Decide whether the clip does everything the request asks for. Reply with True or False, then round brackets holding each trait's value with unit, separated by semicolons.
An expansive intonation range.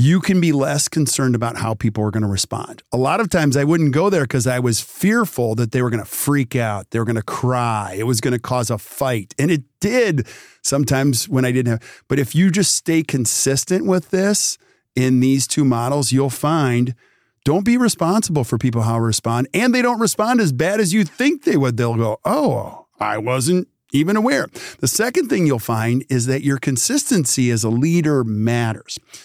True (6.2 semitones)